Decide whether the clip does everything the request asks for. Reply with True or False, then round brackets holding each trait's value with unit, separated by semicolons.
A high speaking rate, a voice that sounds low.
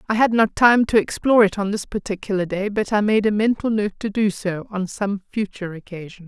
False (230 wpm; 205 Hz)